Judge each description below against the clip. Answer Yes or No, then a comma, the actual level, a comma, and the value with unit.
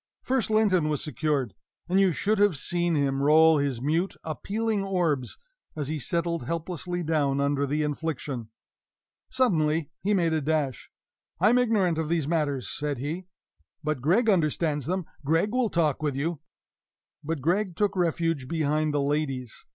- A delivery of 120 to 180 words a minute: Yes, average, 160 wpm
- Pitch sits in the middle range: Yes, medium, 160 Hz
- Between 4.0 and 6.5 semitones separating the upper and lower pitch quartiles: No, average, 3.6 semitones